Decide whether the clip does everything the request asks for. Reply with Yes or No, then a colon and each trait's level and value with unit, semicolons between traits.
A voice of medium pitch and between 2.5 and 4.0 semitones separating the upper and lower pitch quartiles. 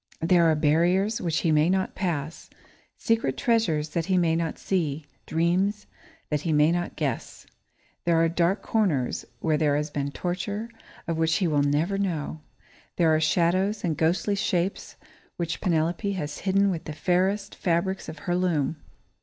Yes: medium, 170 Hz; average, 3.3 semitones